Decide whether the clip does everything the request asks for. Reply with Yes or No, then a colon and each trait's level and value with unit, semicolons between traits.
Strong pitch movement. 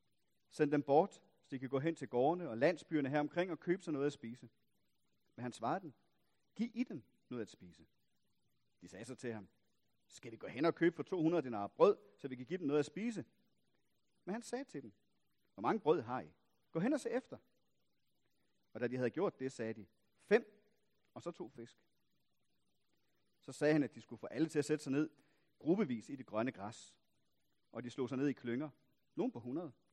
Yes: wide, 5.7 semitones